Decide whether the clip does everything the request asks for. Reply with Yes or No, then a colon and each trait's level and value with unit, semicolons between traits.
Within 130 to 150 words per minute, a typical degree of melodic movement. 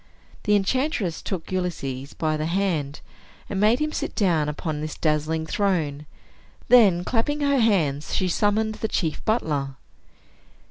No: average, 140 wpm; wide, 5.8 semitones